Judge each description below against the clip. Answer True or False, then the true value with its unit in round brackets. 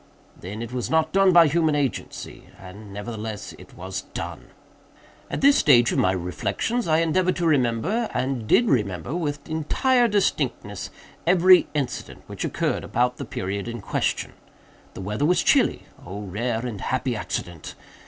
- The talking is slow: False (155 wpm)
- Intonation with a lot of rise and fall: True (8.1 semitones)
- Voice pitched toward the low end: True (125 Hz)